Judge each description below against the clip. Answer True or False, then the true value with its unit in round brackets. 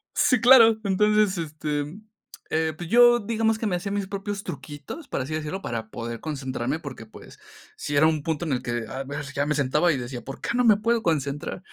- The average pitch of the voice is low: False (155 Hz)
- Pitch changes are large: True (6.7 semitones)